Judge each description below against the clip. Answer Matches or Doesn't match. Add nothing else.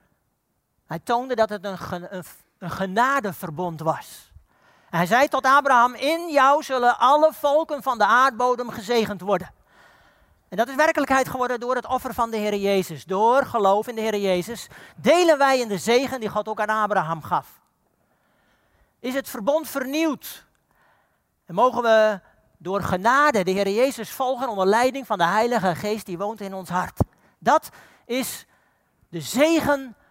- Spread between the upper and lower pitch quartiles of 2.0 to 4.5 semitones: Doesn't match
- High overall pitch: Matches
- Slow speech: Doesn't match